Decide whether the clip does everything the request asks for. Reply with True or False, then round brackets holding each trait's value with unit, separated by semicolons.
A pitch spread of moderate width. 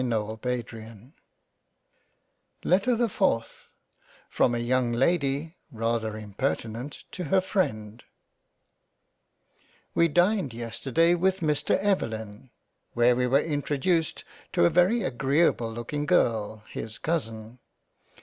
False (6.8 semitones)